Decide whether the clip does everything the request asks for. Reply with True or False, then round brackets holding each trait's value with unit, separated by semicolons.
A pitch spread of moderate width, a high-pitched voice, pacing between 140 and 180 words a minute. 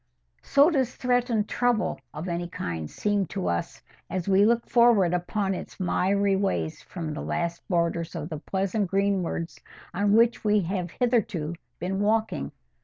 True (4.1 semitones; 195 Hz; 155 wpm)